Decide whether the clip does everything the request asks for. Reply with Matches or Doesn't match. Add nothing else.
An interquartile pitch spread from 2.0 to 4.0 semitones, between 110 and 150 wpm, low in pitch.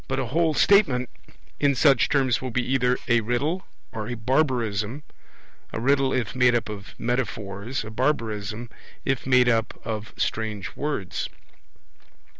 Matches